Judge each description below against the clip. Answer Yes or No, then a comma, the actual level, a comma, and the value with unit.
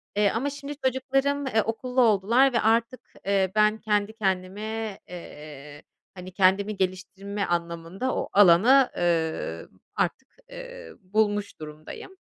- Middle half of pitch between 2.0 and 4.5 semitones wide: No, average, 5.0 semitones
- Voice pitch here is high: Yes, high, 205 Hz